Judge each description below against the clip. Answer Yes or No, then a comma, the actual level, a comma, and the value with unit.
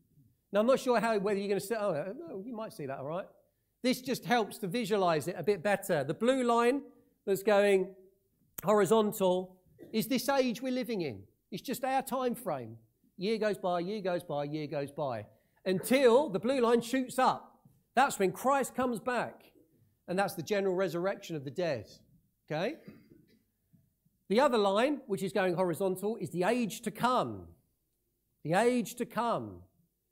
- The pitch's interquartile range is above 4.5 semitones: Yes, average, 5.3 semitones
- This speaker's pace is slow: No, average, 175 wpm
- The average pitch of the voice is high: Yes, high, 200 Hz